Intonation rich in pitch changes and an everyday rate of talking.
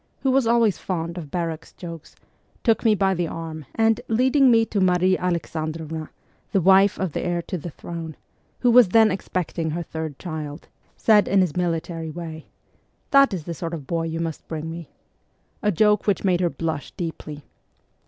No: average, 3.7 semitones; average, 185 wpm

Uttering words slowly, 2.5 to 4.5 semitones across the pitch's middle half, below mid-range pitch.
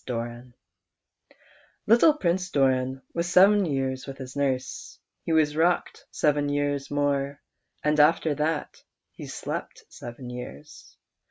No: slow, 120 wpm; average, 3.4 semitones; medium, 145 Hz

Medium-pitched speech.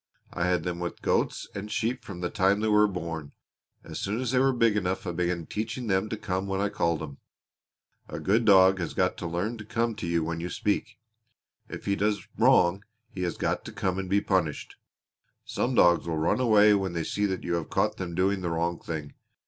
No: very low, 95 Hz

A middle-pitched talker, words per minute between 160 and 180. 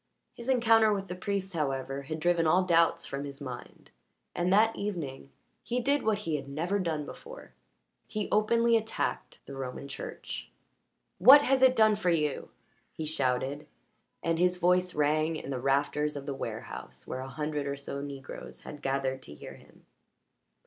Yes: medium, 160 Hz; average, 170 wpm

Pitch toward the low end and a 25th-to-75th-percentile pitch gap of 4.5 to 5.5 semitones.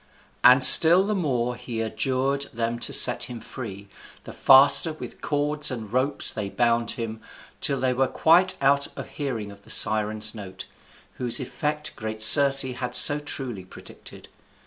No: low, 125 Hz; average, 4.1 semitones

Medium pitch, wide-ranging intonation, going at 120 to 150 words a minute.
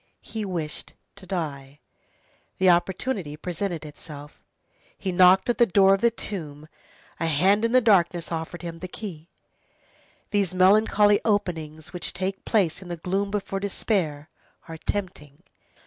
No: medium, 180 Hz; average, 3.8 semitones; average, 145 wpm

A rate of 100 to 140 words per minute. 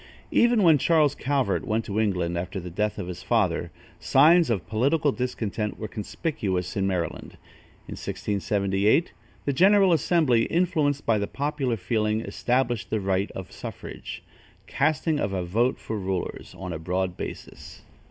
No: average, 150 wpm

